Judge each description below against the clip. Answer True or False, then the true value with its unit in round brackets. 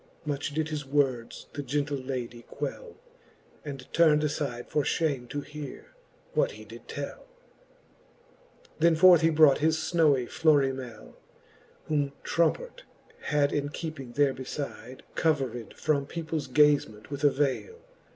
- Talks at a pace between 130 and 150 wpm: True (135 wpm)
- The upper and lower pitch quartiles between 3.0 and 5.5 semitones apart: False (2.6 semitones)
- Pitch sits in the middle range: True (145 Hz)